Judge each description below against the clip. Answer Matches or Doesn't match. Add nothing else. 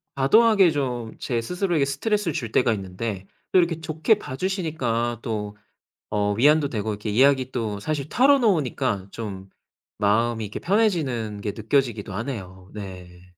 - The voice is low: Matches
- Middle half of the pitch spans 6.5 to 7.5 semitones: Matches